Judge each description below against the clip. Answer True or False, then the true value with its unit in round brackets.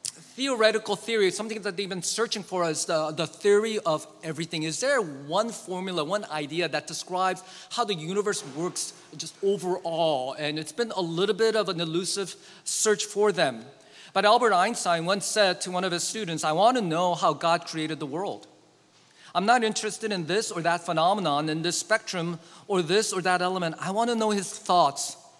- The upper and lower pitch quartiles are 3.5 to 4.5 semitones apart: True (4.1 semitones)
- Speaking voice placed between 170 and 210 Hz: True (185 Hz)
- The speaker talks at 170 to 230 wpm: True (190 wpm)